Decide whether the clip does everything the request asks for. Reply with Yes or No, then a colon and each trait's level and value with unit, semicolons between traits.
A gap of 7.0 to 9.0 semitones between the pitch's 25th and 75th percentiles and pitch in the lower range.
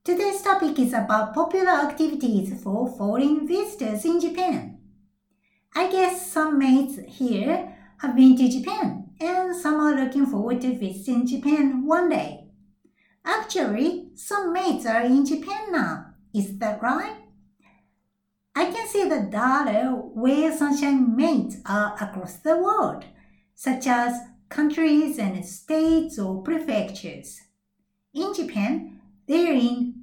No: wide, 7.3 semitones; very high, 265 Hz